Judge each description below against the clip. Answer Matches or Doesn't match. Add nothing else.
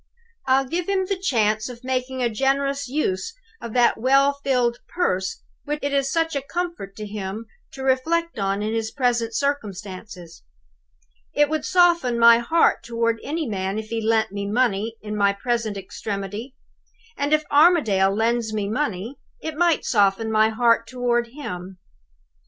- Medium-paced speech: Matches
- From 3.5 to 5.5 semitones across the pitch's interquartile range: Matches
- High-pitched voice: Matches